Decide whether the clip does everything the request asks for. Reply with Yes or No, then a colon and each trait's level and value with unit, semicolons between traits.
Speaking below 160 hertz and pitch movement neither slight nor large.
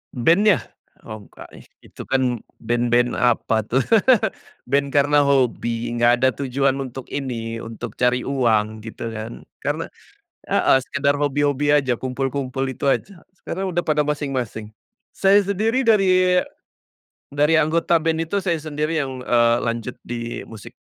Yes: low, 135 Hz; average, 4.2 semitones